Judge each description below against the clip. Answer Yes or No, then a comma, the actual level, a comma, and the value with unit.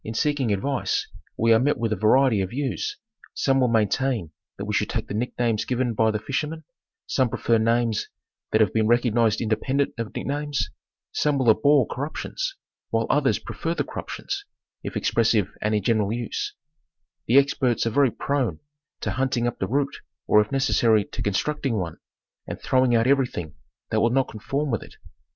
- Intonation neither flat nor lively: Yes, average, 3.9 semitones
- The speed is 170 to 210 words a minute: Yes, average, 190 wpm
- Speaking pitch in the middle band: No, low, 120 Hz